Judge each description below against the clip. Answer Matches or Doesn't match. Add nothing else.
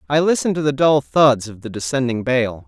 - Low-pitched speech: Matches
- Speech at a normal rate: Doesn't match